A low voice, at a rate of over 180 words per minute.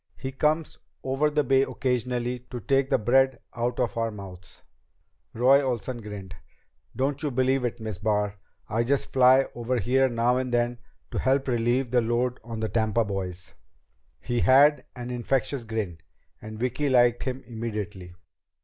No: low, 120 Hz; average, 160 wpm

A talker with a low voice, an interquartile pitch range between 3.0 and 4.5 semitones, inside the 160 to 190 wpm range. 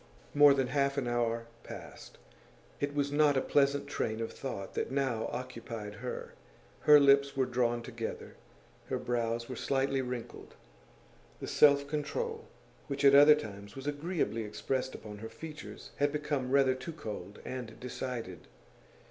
No: low, 130 Hz; average, 3.5 semitones; average, 150 wpm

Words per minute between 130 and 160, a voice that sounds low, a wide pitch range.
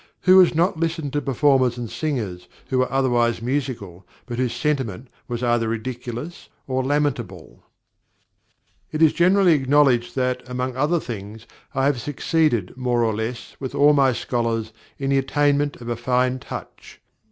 No: average, 155 wpm; low, 130 Hz; average, 3.5 semitones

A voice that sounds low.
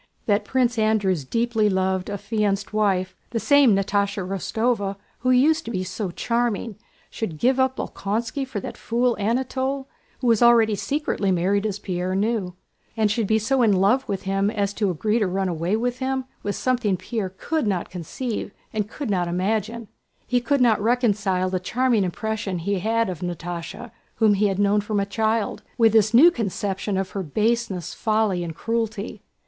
No: high, 210 Hz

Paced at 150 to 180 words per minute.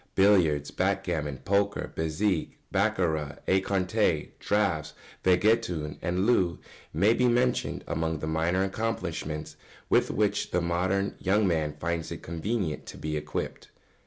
No: slow, 135 wpm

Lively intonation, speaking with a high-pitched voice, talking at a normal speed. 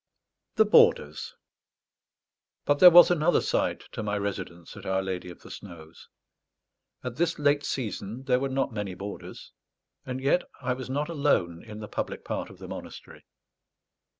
No: wide, 6.5 semitones; low, 125 Hz; average, 160 wpm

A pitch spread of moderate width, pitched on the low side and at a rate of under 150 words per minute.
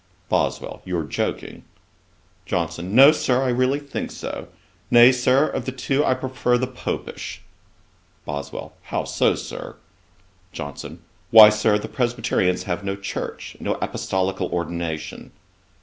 No: wide, 6.8 semitones; low, 105 Hz; slow, 135 wpm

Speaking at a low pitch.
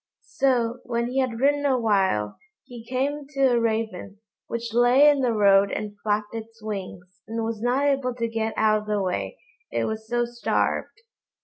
No: high, 230 Hz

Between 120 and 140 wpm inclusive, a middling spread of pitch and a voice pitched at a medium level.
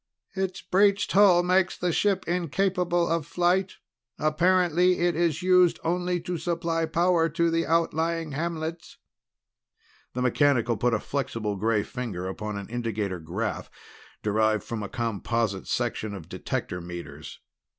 No: slow, 135 wpm; wide, 7.6 semitones; medium, 165 Hz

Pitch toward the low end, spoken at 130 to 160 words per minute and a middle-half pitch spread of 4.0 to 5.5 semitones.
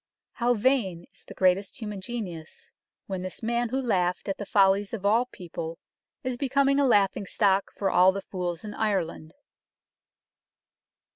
No: high, 200 Hz; average, 155 wpm; average, 4.4 semitones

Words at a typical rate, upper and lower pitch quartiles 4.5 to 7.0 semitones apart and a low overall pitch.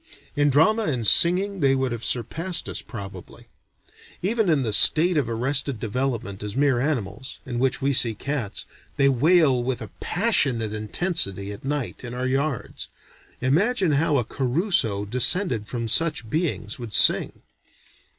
Yes: average, 150 wpm; average, 5.3 semitones; low, 130 Hz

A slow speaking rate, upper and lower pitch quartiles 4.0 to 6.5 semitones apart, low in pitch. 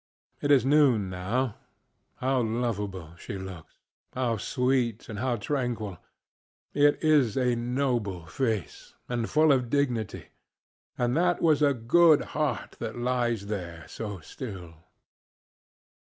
Yes: slow, 125 wpm; average, 4.5 semitones; low, 120 Hz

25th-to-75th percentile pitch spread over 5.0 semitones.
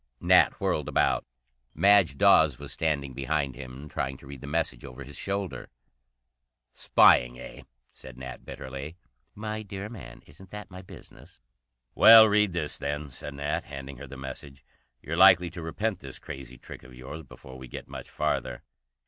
Yes: wide, 5.6 semitones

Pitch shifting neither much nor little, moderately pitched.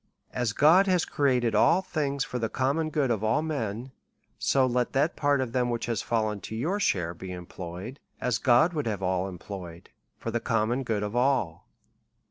No: average, 5.0 semitones; low, 120 Hz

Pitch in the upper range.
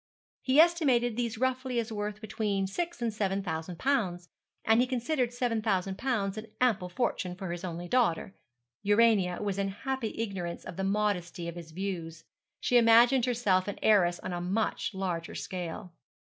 Yes: high, 205 Hz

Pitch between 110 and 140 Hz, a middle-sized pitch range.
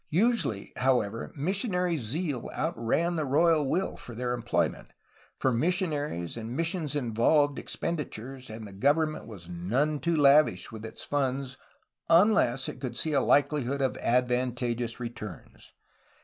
Yes: low, 135 Hz; average, 5.0 semitones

